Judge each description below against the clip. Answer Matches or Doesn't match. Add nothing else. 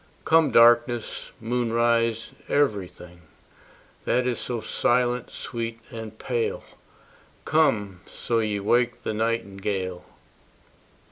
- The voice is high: Doesn't match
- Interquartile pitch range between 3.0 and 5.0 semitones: Doesn't match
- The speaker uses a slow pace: Matches